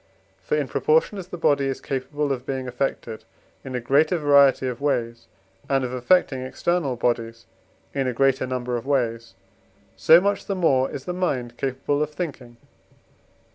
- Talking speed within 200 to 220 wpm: No, average, 175 wpm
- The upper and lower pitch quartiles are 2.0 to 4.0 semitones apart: Yes, average, 3.3 semitones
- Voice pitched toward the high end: No, low, 135 Hz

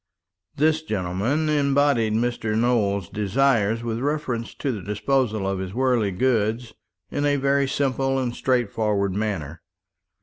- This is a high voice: No, low, 120 Hz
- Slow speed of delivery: Yes, slow, 130 wpm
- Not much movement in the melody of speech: No, average, 4.7 semitones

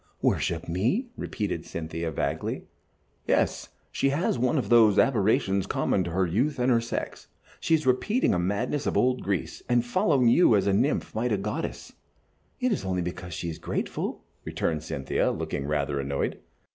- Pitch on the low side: Yes, low, 105 Hz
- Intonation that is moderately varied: No, wide, 6.6 semitones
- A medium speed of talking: Yes, average, 170 wpm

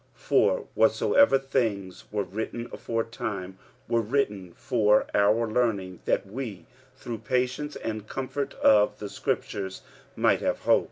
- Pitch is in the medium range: No, low, 110 Hz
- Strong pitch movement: No, average, 3.8 semitones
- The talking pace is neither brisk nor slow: No, slow, 130 wpm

